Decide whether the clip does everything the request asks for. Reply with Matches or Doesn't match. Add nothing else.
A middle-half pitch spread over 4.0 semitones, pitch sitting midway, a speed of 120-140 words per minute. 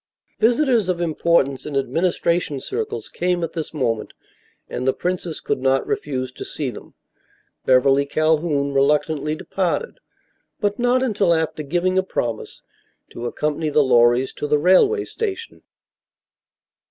Matches